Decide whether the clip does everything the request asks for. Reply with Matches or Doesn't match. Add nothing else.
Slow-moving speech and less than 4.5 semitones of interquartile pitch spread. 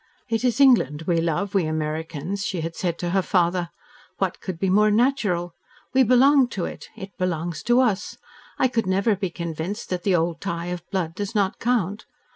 Doesn't match